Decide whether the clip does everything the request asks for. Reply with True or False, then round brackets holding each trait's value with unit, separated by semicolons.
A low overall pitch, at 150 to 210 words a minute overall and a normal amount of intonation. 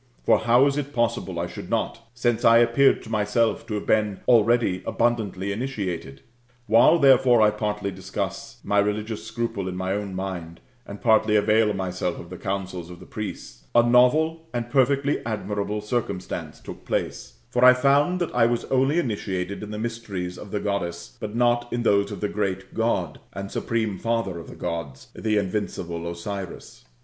True (105 Hz; 175 wpm; 3.8 semitones)